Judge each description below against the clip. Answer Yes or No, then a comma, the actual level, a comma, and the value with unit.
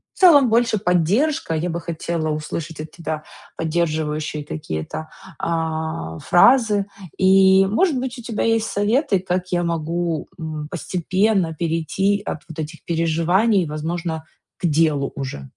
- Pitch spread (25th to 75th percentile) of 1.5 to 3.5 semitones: No, average, 3.9 semitones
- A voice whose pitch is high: No, medium, 170 Hz